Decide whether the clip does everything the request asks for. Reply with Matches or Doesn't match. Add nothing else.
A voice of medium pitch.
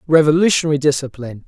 Matches